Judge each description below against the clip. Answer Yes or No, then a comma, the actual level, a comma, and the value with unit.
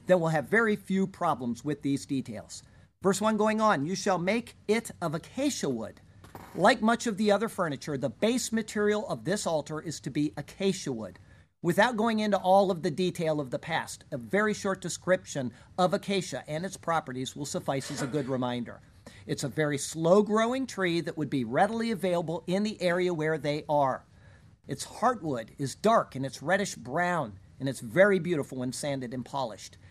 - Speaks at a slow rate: No, average, 190 wpm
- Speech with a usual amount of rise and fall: No, wide, 5.8 semitones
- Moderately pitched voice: Yes, medium, 165 Hz